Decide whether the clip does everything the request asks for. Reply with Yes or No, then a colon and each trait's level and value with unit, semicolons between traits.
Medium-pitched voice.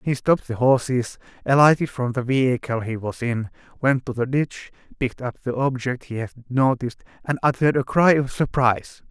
No: low, 125 Hz